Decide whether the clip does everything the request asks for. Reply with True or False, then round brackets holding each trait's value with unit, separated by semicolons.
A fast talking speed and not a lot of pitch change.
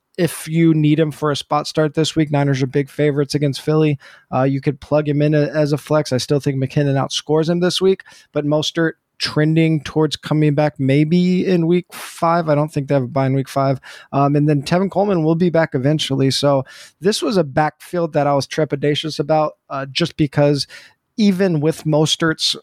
True (210 wpm; 2.1 semitones)